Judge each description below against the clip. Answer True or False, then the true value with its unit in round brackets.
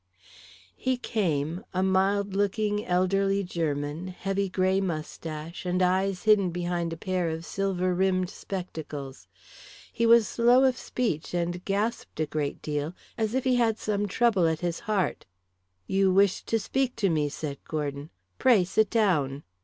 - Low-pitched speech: False (185 Hz)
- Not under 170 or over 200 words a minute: False (155 wpm)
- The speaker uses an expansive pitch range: False (3.9 semitones)